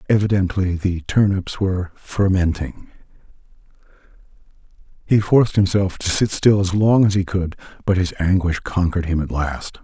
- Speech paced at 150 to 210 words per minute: No, average, 140 wpm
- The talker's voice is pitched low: Yes, very low, 90 Hz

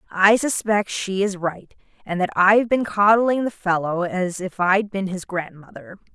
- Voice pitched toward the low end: No, high, 190 Hz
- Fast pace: No, average, 175 wpm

